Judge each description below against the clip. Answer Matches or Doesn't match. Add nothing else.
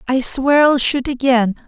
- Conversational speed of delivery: Matches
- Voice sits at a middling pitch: Doesn't match